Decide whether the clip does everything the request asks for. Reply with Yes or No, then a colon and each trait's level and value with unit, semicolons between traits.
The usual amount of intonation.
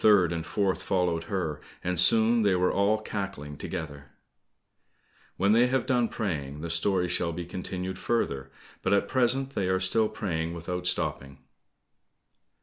Yes: average, 3.9 semitones